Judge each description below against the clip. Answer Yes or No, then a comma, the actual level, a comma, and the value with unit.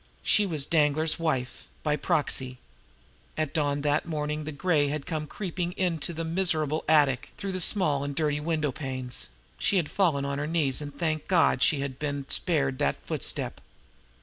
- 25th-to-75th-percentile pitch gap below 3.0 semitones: Yes, narrow, 2.6 semitones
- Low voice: No, medium, 150 Hz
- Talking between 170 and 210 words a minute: Yes, average, 175 wpm